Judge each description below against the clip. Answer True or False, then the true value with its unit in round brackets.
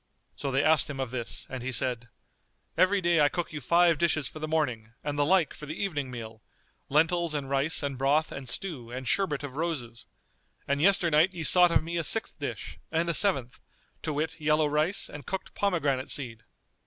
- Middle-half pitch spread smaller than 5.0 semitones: True (4.1 semitones)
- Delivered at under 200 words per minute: False (205 wpm)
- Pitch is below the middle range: False (150 Hz)